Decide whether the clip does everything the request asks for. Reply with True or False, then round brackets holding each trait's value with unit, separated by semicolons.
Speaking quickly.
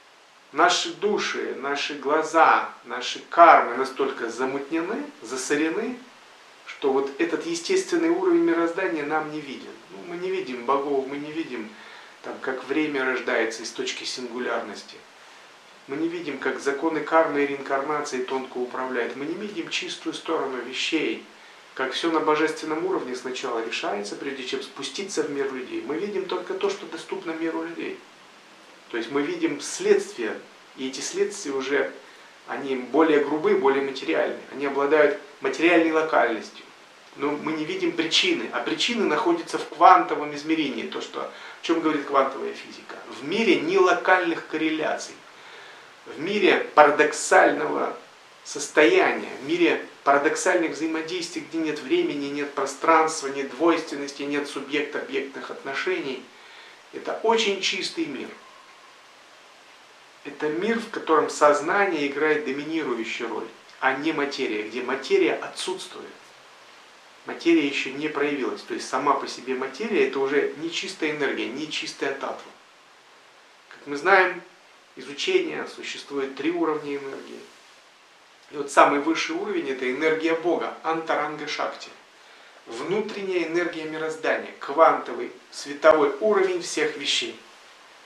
False (130 wpm)